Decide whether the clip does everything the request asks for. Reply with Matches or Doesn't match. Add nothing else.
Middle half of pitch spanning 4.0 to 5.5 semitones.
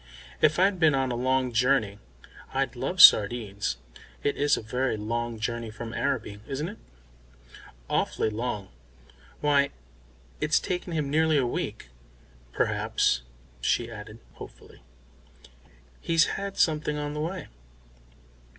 Matches